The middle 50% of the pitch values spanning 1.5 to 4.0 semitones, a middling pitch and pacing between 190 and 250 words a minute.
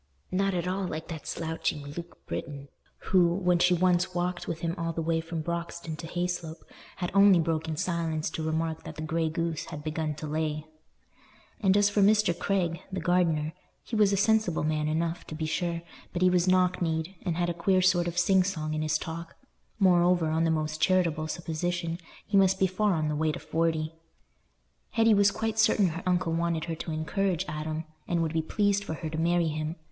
Yes: narrow, 2.5 semitones; medium, 170 Hz; fast, 205 wpm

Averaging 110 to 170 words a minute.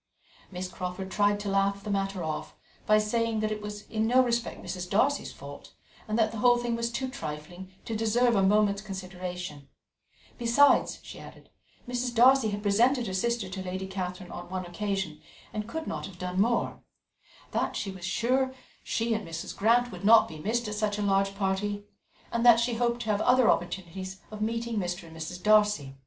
No: average, 195 wpm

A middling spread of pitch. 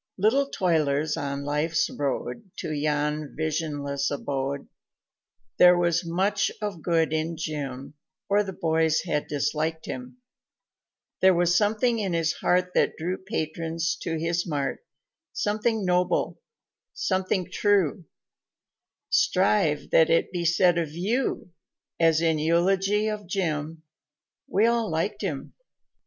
Yes: average, 3.8 semitones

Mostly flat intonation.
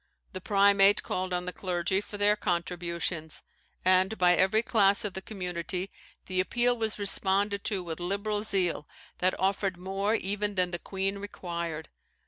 Yes: narrow, 2.2 semitones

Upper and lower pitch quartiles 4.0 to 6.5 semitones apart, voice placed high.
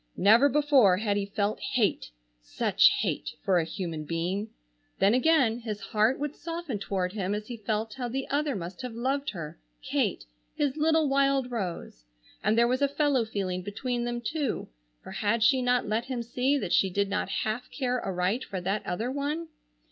Yes: average, 5.1 semitones; high, 230 Hz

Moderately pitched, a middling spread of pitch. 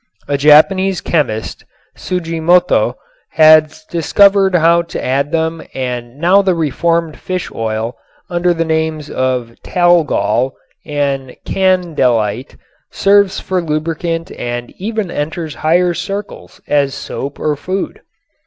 Yes: medium, 160 Hz; average, 4.0 semitones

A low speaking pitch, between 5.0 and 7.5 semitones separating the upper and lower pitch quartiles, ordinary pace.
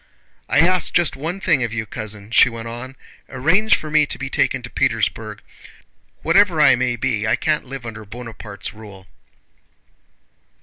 Yes: low, 125 Hz; wide, 5.6 semitones; average, 165 wpm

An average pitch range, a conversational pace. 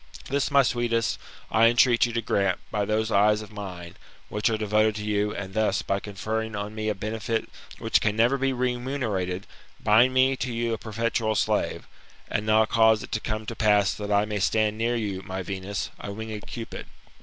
No: narrow, 2.1 semitones; average, 190 wpm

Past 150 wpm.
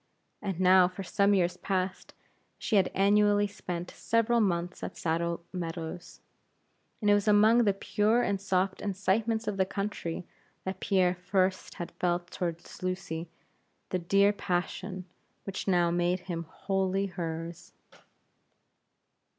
No: slow, 135 wpm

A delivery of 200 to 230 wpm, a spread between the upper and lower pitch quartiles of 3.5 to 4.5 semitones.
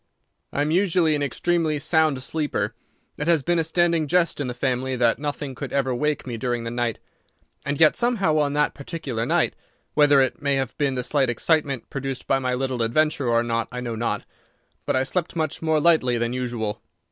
Yes: fast, 205 wpm; average, 3.9 semitones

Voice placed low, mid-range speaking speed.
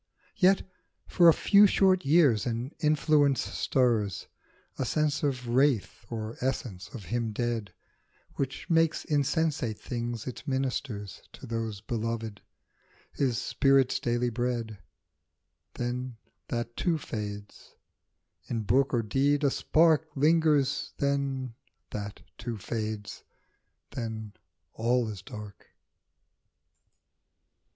No: low, 125 Hz; slow, 110 wpm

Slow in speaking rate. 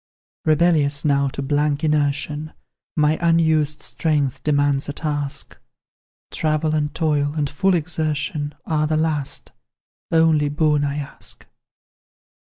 Yes: slow, 115 wpm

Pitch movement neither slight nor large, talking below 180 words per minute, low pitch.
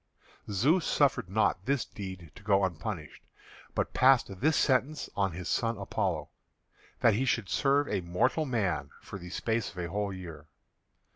No: wide, 5.9 semitones; average, 160 wpm; low, 100 Hz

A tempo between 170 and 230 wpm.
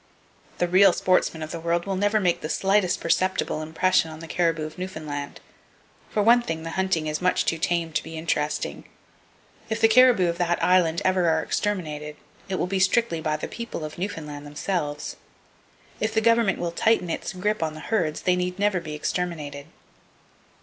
Yes: average, 185 wpm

